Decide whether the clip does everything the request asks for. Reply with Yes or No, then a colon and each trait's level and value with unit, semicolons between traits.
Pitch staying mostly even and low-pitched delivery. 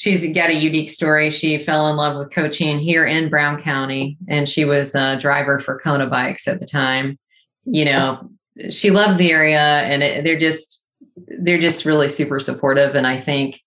No: narrow, 2.3 semitones; medium, 150 Hz